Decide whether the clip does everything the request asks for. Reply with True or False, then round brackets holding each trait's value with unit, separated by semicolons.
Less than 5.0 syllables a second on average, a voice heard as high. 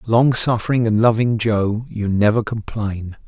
False (4.3 syllables/s; 110 Hz)